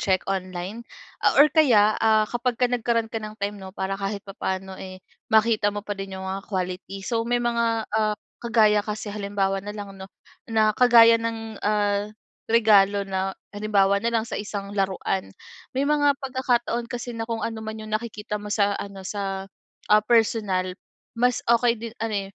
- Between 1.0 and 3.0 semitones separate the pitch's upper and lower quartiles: Yes, average, 2.7 semitones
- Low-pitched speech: No, high, 215 Hz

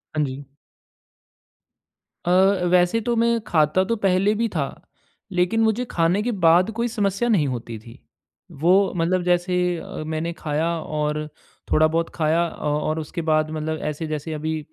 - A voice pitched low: No, medium, 165 Hz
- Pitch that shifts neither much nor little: Yes, average, 3.3 semitones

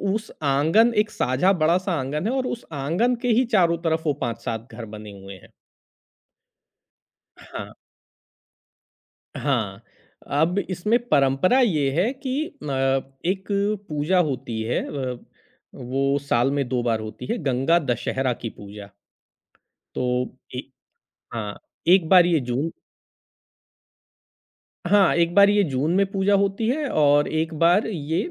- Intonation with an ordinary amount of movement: No, wide, 7.1 semitones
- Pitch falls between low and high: Yes, medium, 155 Hz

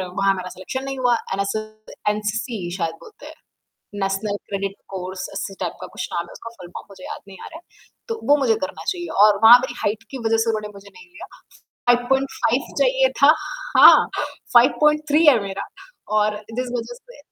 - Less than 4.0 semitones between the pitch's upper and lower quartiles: No, wide, 5.5 semitones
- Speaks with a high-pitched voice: Yes, high, 215 Hz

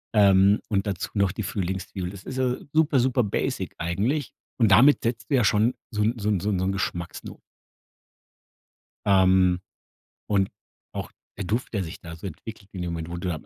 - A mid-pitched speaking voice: No, low, 100 Hz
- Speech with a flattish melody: No, average, 3.6 semitones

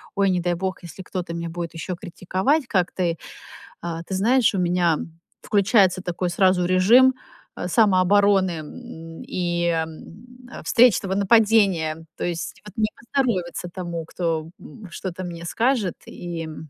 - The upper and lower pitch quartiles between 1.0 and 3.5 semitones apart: Yes, average, 2.9 semitones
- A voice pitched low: No, medium, 185 Hz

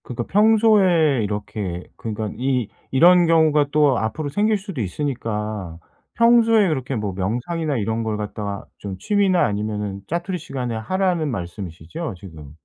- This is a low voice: Yes, low, 125 Hz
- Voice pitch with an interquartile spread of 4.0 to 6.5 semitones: No, wide, 8.7 semitones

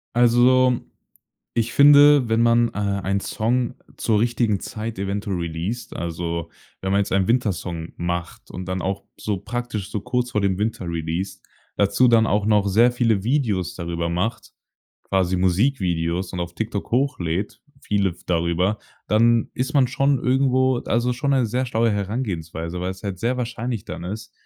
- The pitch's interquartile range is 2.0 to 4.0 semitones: No, average, 4.7 semitones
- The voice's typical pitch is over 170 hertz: No, low, 105 Hz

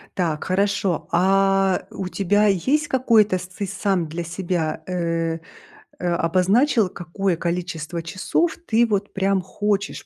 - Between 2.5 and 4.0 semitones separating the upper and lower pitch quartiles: Yes, average, 2.8 semitones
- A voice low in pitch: No, high, 190 Hz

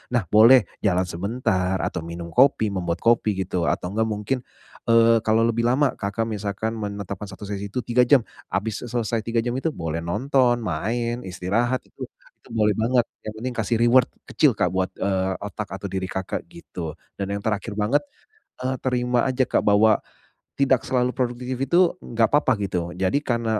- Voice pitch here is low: Yes, low, 110 Hz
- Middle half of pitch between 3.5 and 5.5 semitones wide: Yes, average, 4.0 semitones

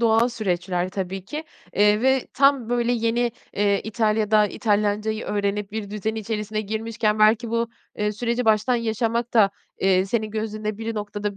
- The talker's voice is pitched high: Yes, high, 215 Hz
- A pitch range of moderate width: No, narrow, 1.9 semitones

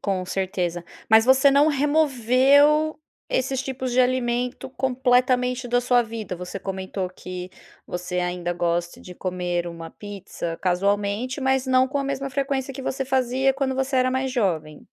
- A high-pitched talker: Yes, high, 245 Hz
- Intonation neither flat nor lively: No, wide, 6.3 semitones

